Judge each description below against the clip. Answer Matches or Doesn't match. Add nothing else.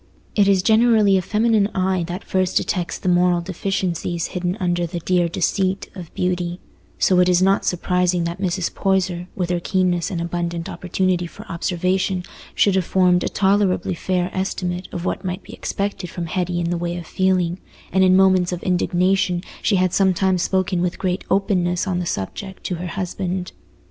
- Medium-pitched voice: Matches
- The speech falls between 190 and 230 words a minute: Doesn't match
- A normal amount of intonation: Doesn't match